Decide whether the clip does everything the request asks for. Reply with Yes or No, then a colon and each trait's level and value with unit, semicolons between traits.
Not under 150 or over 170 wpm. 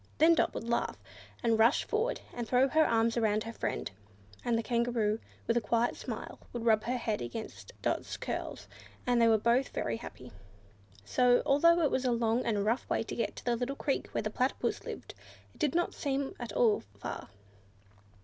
No: average, 195 wpm